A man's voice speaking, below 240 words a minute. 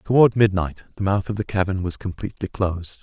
Yes: male; average, 200 wpm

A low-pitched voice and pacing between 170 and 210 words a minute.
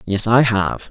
Yes: low, 110 Hz; average, 200 wpm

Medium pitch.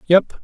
Yes: medium, 180 Hz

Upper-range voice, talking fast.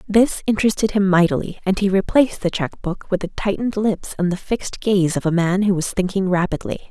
Yes: high, 195 Hz; fast, 215 wpm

